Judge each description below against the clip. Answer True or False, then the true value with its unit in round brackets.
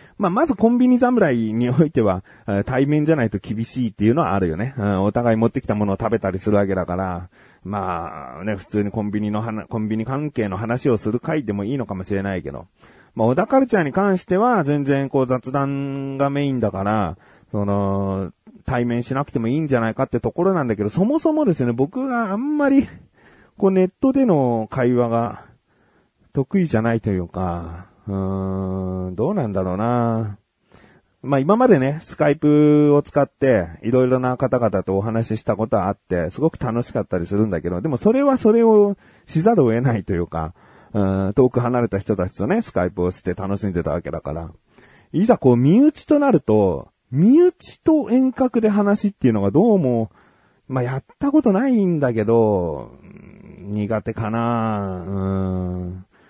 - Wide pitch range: True (6.7 semitones)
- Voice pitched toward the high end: False (115 Hz)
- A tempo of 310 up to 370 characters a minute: True (360 characters per minute)